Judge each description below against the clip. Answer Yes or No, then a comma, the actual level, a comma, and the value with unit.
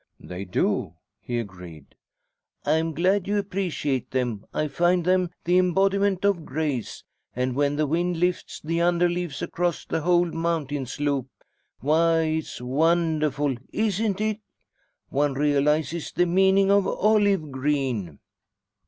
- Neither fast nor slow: No, slow, 130 wpm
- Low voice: No, medium, 160 Hz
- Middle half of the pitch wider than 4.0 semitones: Yes, average, 4.4 semitones